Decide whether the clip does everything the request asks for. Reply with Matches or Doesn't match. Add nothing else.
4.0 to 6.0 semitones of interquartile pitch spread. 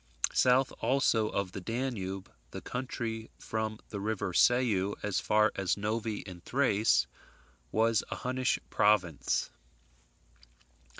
Doesn't match